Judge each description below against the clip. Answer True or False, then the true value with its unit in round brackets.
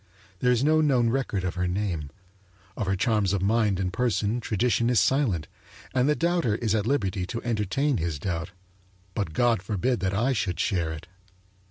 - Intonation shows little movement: False (5.0 semitones)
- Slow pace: False (185 wpm)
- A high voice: False (105 Hz)